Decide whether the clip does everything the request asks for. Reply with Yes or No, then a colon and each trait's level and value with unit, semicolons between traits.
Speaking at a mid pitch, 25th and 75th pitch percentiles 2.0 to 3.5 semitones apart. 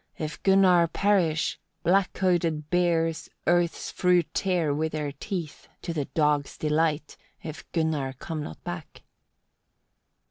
Yes: medium, 165 Hz; narrow, 2.6 semitones